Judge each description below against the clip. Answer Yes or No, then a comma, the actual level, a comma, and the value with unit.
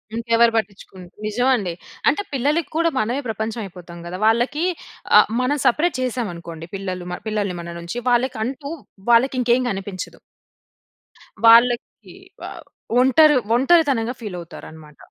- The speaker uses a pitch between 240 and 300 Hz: No, high, 230 Hz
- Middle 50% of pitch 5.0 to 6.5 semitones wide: Yes, average, 5.3 semitones